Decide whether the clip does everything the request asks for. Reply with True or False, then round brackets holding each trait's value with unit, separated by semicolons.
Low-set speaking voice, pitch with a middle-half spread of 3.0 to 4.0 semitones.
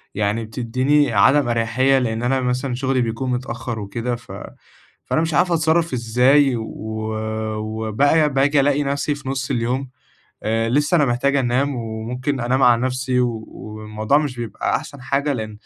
True (125 Hz; 3.3 semitones)